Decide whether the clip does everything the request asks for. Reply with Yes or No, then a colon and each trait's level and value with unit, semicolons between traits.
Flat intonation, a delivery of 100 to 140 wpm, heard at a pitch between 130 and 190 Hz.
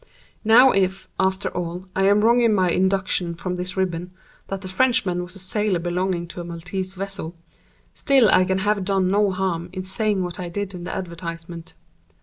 No: narrow, 1.9 semitones; average, 190 wpm; medium, 185 Hz